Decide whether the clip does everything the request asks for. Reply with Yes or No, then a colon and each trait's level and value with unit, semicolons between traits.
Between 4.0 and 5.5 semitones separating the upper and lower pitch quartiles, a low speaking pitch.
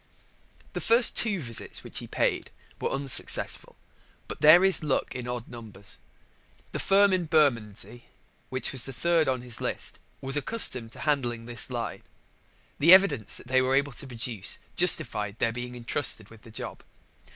Yes: average, 4.7 semitones; low, 130 Hz